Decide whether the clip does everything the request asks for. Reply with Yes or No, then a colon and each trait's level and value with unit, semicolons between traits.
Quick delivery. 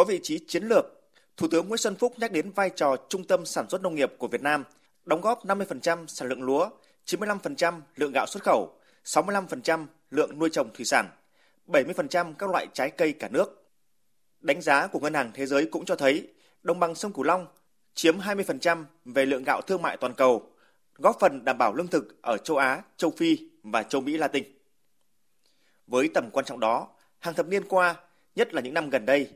No: average, 205 wpm